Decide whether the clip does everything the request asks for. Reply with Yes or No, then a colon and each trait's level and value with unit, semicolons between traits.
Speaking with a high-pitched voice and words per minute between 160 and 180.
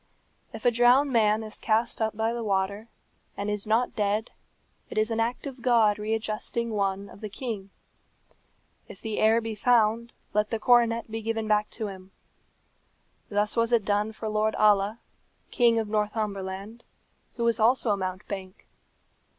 Yes: high, 220 Hz; average, 165 wpm